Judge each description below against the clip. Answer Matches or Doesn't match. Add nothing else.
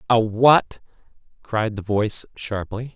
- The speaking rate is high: Doesn't match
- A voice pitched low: Matches